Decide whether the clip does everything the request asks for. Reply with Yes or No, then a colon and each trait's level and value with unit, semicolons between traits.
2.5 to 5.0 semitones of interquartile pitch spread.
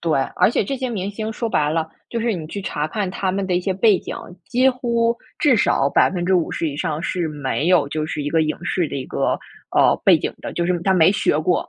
No: wide, 5.5 semitones